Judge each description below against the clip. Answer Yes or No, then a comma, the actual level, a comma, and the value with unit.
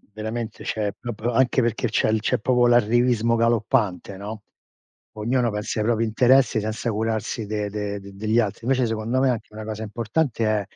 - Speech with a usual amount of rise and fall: No, narrow, 2.0 semitones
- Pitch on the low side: Yes, low, 110 Hz